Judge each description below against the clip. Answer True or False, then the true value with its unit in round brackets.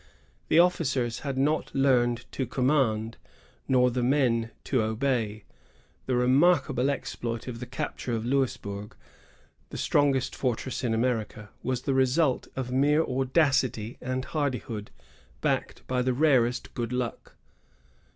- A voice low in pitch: True (125 Hz)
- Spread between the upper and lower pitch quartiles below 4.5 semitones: True (2.5 semitones)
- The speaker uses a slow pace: True (130 wpm)